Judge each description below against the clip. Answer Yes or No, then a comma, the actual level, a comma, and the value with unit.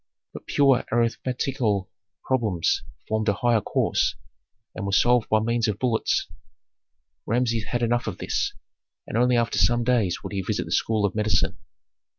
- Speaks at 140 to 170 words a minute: Yes, average, 160 wpm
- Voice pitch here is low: Yes, low, 115 Hz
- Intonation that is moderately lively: No, narrow, 2.3 semitones